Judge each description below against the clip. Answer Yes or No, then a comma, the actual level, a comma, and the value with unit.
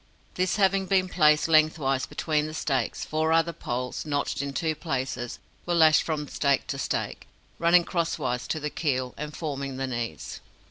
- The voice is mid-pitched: Yes, medium, 150 Hz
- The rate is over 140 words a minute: Yes, average, 170 wpm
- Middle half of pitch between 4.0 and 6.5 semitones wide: No, average, 3.5 semitones